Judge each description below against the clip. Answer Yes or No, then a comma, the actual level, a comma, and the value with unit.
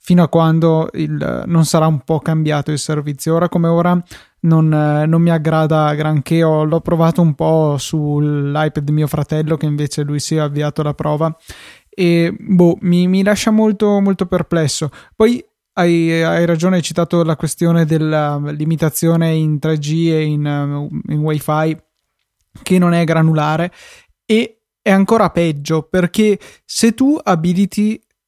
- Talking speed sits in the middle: Yes, average, 150 wpm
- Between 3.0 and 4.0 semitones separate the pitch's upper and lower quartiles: No, narrow, 2.4 semitones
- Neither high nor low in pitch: Yes, medium, 160 Hz